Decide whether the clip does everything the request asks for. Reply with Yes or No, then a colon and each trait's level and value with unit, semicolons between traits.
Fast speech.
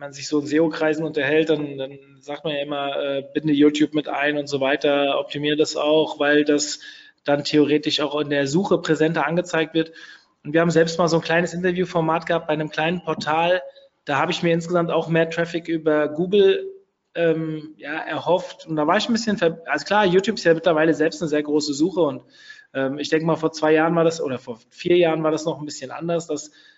Yes: fast, 230 wpm